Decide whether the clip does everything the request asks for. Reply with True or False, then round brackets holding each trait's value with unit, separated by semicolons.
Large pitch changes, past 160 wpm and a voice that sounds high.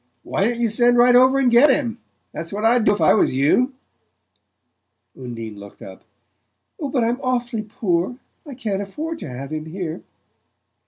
True (6.8 semitones; 170 wpm; 225 Hz)